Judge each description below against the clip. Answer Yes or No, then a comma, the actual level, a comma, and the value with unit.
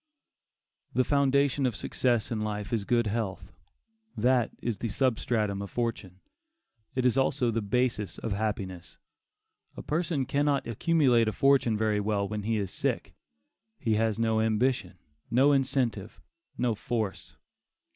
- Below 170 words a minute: Yes, average, 145 wpm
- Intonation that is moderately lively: Yes, average, 3.5 semitones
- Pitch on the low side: Yes, low, 115 Hz